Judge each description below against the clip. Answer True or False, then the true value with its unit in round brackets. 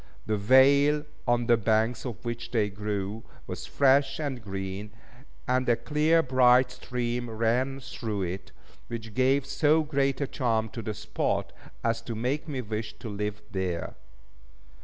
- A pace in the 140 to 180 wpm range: True (155 wpm)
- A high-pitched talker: False (120 Hz)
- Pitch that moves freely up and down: False (3.6 semitones)